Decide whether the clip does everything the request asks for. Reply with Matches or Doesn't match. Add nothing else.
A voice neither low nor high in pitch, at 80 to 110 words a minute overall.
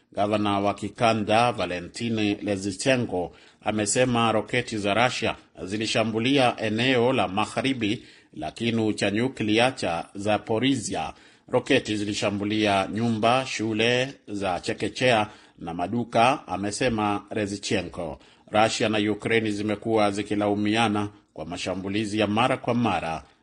Doesn't match